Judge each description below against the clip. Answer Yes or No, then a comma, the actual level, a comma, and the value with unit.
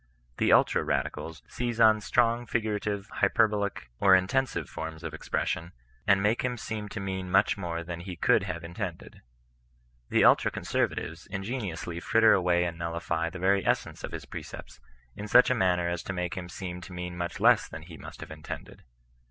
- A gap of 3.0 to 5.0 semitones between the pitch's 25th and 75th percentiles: Yes, average, 3.4 semitones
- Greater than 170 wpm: Yes, average, 180 wpm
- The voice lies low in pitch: Yes, very low, 95 Hz